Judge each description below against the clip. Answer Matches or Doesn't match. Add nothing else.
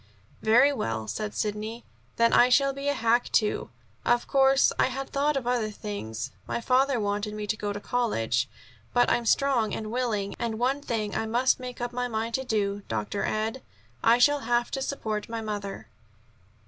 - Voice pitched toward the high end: Matches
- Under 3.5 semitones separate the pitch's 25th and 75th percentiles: Matches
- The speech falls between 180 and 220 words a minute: Matches